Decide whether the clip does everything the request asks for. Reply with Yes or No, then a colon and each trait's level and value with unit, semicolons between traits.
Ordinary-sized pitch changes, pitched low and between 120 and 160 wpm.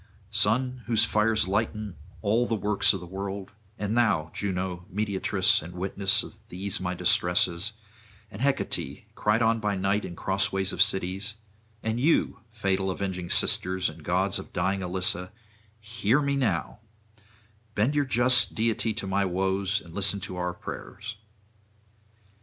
Yes: average, 3.0 semitones; low, 100 Hz; average, 145 wpm